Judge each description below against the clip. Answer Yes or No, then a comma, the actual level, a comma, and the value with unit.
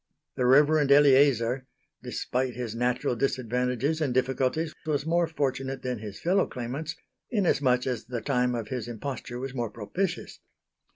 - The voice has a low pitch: Yes, low, 130 Hz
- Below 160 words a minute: Yes, average, 140 wpm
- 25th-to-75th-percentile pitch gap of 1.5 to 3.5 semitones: Yes, average, 2.9 semitones